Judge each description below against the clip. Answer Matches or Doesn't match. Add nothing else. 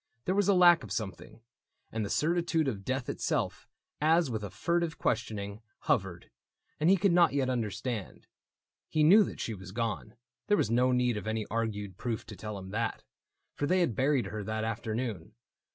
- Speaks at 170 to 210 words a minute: Matches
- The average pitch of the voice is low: Matches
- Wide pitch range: Matches